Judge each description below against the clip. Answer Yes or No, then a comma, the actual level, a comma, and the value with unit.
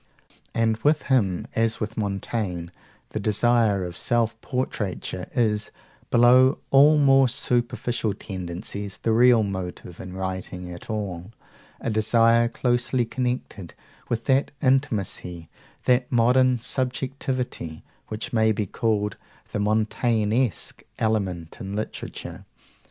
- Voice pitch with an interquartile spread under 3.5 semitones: No, average, 3.9 semitones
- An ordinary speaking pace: No, slow, 115 wpm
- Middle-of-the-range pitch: No, low, 110 Hz